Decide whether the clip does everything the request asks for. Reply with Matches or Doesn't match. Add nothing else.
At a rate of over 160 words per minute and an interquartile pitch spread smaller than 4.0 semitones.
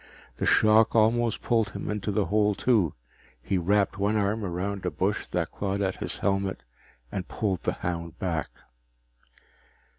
Doesn't match